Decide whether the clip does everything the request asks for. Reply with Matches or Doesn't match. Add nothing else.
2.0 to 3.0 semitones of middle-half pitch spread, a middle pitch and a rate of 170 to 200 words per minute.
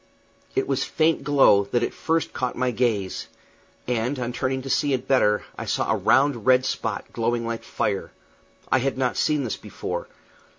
Doesn't match